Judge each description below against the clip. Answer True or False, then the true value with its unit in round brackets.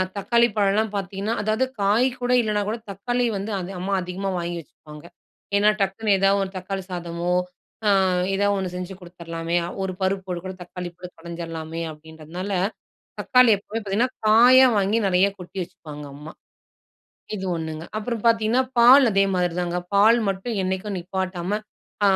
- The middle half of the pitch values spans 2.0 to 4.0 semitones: True (3.4 semitones)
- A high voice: True (195 Hz)